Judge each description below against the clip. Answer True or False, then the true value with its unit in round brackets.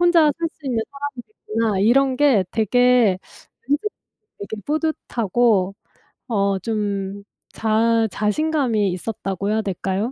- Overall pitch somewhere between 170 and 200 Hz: False (225 Hz)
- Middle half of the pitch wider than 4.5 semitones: True (5.2 semitones)